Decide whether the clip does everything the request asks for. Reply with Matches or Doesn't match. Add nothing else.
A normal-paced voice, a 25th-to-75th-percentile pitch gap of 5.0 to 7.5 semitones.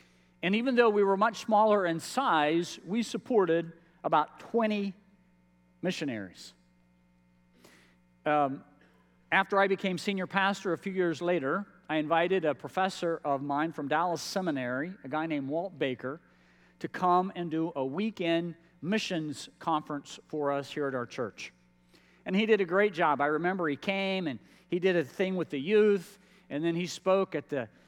Matches